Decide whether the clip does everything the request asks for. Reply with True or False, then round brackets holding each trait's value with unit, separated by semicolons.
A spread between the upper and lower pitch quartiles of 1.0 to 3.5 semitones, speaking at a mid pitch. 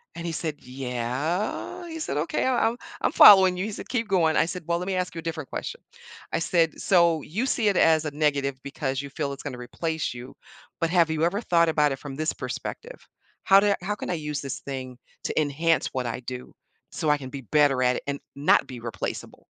False (4.6 semitones; 155 Hz)